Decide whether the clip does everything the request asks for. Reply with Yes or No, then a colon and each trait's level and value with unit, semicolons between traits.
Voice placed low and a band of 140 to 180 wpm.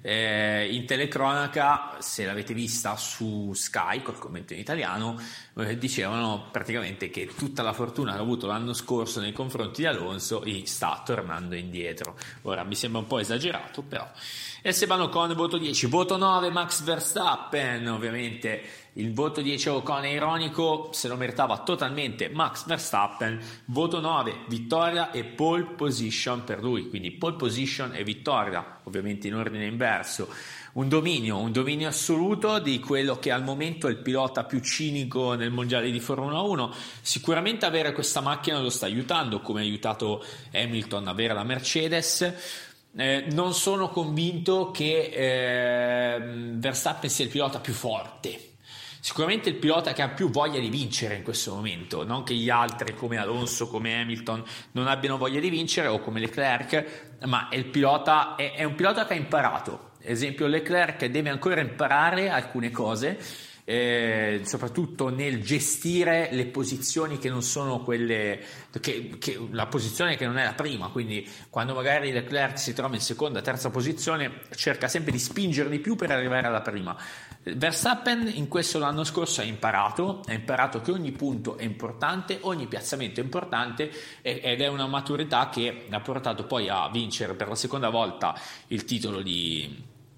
Yes: low, 130 Hz; average, 160 wpm